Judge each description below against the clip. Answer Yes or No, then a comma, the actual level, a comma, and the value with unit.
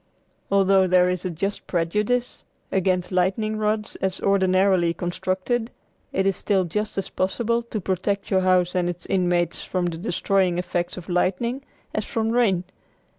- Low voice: No, high, 190 Hz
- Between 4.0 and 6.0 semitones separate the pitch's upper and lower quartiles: No, average, 2.7 semitones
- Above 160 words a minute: No, average, 155 wpm